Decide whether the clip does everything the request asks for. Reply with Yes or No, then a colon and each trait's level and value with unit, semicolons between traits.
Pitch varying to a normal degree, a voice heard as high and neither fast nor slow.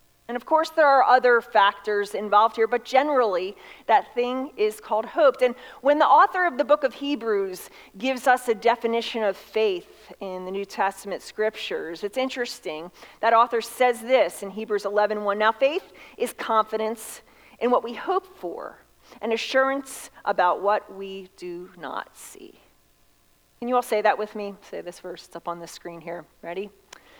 Yes: average, 4.6 semitones; high, 230 Hz; average, 175 wpm